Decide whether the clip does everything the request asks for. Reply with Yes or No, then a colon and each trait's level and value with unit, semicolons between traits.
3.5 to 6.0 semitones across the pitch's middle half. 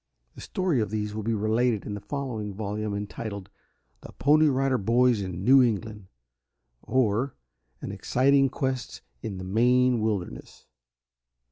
Yes: average, 3.8 semitones